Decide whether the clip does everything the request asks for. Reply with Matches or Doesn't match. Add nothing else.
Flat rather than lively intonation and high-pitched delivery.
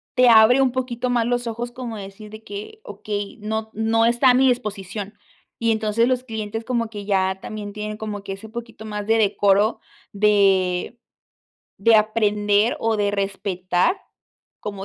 Matches